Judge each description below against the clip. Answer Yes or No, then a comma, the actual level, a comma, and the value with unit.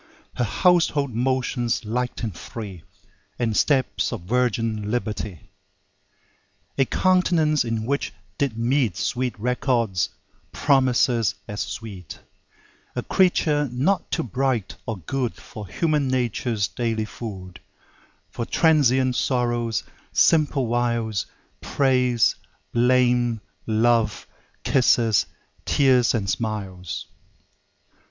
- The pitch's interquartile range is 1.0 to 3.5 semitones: Yes, average, 3.1 semitones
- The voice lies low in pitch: Yes, low, 120 Hz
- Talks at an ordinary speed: No, slow, 100 wpm